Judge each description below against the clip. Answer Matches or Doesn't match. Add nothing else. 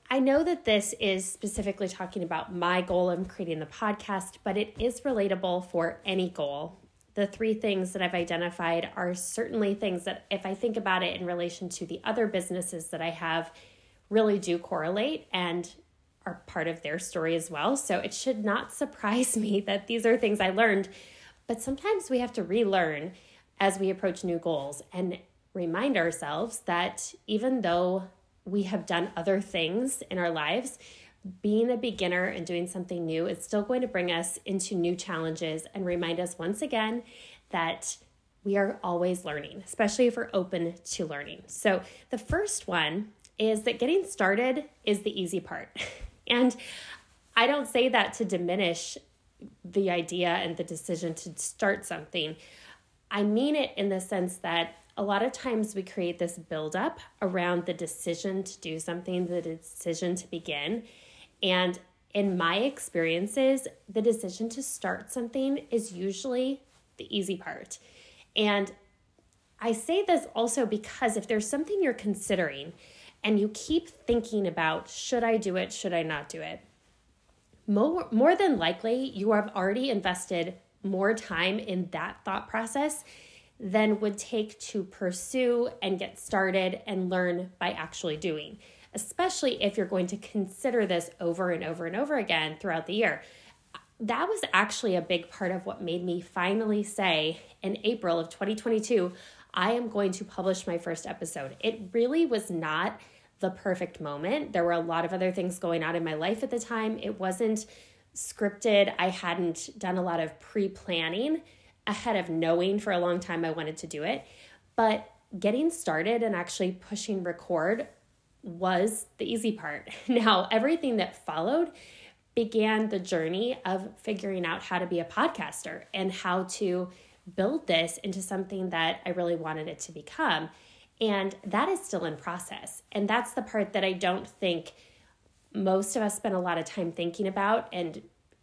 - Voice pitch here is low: Doesn't match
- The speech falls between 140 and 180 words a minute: Matches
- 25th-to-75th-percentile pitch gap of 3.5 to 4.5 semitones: Matches